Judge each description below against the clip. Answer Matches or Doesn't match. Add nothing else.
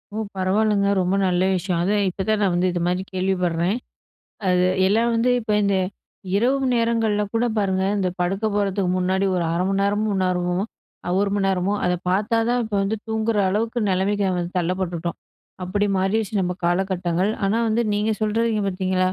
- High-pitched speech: Matches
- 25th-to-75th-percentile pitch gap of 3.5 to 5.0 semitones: Doesn't match